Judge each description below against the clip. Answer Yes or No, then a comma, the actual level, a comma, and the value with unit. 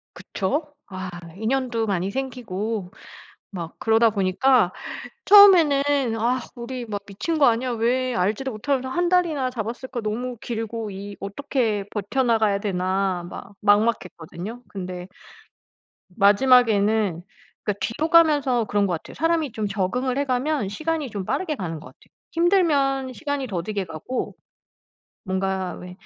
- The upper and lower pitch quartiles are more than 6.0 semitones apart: No, average, 5.2 semitones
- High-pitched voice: Yes, high, 230 Hz